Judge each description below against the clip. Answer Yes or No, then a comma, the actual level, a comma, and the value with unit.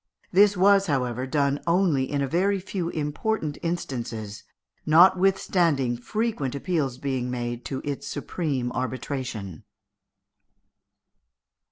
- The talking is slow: Yes, slow, 100 wpm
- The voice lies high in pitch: No, medium, 145 Hz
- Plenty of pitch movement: Yes, wide, 6.0 semitones